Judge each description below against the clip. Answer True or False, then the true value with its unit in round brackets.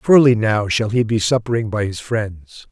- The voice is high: False (110 Hz)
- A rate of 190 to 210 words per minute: True (200 wpm)